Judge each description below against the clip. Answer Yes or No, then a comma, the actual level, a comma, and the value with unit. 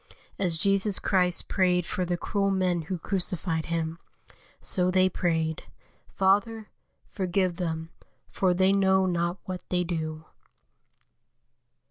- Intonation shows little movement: Yes, narrow, 2.1 semitones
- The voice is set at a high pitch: No, medium, 180 Hz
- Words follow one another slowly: Yes, slow, 120 wpm